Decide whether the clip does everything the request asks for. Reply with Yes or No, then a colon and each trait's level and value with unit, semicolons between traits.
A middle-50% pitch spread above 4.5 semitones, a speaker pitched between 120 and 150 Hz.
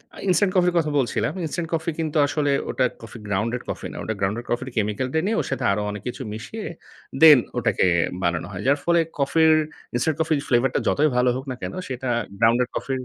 Yes: wide, 5.4 semitones; low, 135 Hz